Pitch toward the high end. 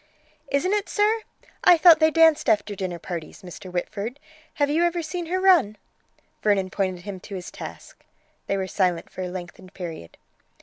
Yes: high, 205 Hz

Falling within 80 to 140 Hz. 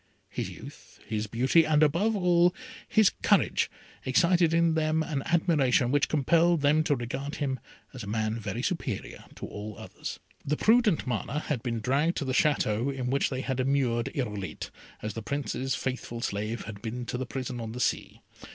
Yes: low, 135 Hz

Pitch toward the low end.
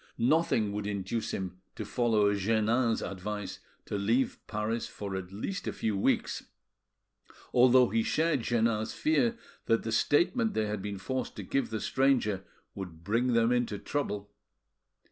Yes: low, 110 Hz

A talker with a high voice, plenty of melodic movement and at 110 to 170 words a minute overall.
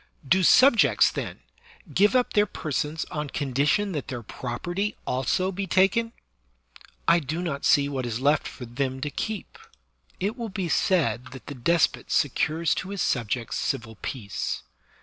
No: medium, 150 Hz; wide, 6.6 semitones; average, 160 wpm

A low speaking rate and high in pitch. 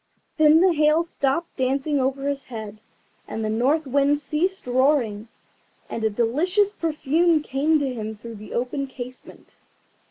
No: average, 150 wpm; very high, 275 Hz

